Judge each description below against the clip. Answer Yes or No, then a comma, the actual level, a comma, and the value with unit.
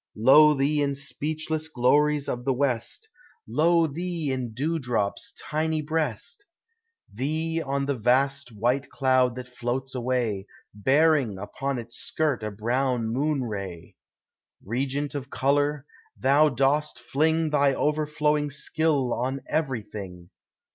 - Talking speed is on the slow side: Yes, slow, 120 wpm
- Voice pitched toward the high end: No, medium, 140 Hz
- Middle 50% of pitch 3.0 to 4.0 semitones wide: Yes, average, 3.6 semitones